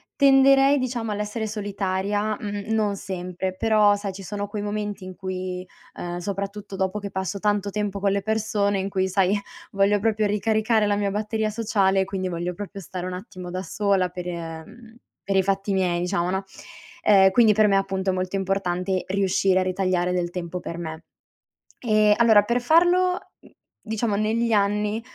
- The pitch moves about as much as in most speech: No, narrow, 2.2 semitones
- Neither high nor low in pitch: No, high, 200 Hz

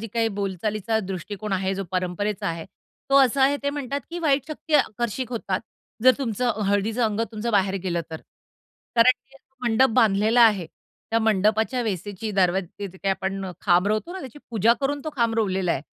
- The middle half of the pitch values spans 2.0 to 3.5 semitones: No, average, 4.2 semitones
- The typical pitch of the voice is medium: No, high, 215 Hz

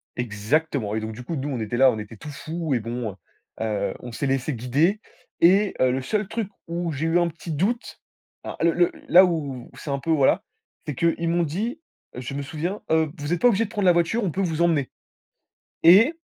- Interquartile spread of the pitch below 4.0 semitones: No, average, 5.3 semitones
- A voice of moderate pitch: Yes, medium, 160 Hz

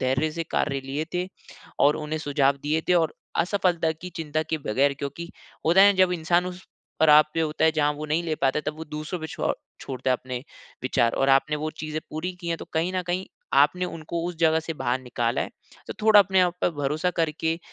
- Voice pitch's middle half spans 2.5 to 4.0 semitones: Yes, average, 2.8 semitones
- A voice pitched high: No, medium, 155 Hz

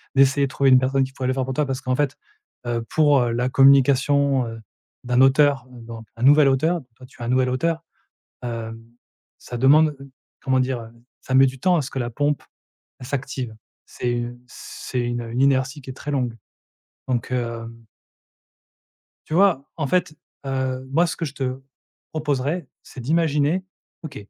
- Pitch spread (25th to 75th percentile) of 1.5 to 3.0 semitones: Yes, narrow, 2.5 semitones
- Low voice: Yes, low, 130 Hz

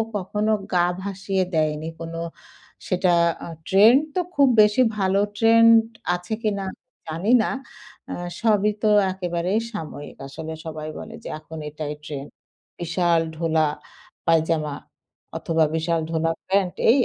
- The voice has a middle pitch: Yes, medium, 175 Hz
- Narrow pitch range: No, average, 3.9 semitones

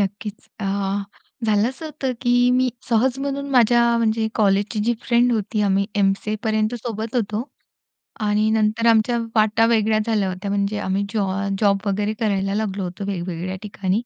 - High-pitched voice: Yes, high, 215 Hz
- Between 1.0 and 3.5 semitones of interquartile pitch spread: Yes, average, 2.7 semitones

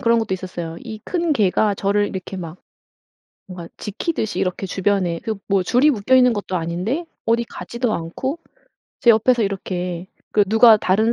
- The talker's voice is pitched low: No, high, 205 Hz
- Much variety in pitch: No, average, 4.1 semitones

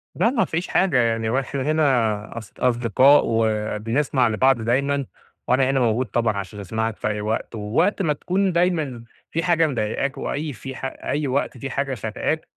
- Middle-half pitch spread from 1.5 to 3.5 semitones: No, average, 4.6 semitones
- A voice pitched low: Yes, low, 130 Hz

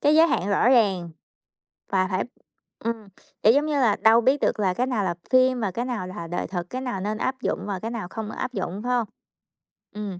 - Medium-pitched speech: No, high, 220 Hz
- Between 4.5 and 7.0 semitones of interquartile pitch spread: Yes, average, 4.8 semitones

